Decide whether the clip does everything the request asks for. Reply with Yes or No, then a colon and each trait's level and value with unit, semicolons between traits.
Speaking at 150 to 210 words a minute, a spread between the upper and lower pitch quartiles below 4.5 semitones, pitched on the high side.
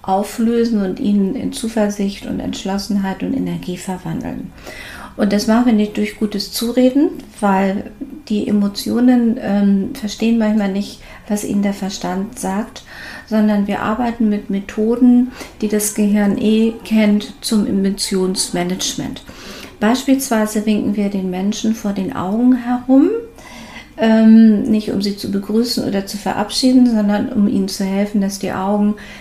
No: average, 140 wpm; narrow, 2.4 semitones; high, 210 Hz